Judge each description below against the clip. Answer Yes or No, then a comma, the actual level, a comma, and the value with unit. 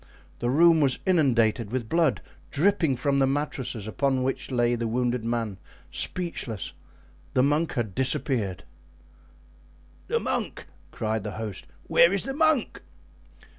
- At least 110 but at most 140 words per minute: Yes, slow, 135 wpm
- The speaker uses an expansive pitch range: No, average, 5.0 semitones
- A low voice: Yes, low, 130 Hz